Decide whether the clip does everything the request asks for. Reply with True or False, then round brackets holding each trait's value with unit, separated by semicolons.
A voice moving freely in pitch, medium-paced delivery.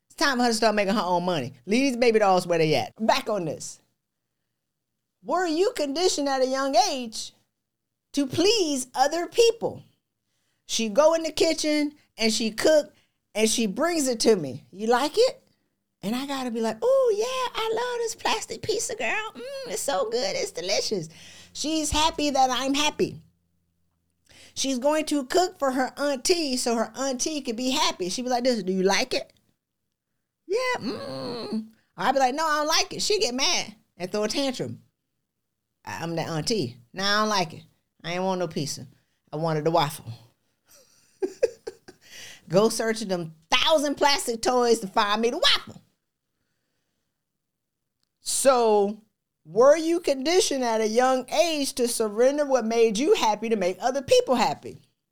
True (8.0 semitones; 170 wpm)